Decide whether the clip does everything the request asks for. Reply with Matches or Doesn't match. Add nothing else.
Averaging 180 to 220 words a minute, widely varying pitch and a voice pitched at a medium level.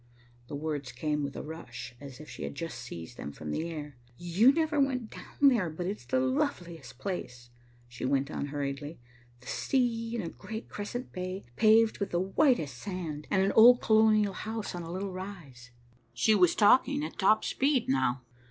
Matches